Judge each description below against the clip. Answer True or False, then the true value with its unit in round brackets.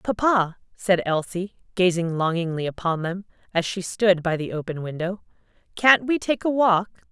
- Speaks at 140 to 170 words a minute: True (160 wpm)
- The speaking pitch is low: False (185 Hz)